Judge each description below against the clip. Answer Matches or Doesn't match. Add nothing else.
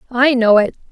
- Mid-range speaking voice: Doesn't match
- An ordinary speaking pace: Matches